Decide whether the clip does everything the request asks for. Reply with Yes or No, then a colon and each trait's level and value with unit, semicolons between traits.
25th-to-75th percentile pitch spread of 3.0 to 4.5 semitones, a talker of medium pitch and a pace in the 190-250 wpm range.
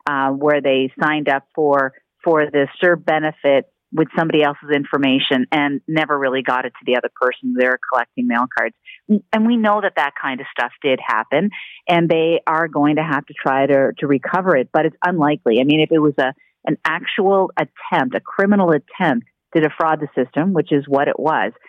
Yes: average, 3.5 semitones; medium, 150 Hz; average, 200 wpm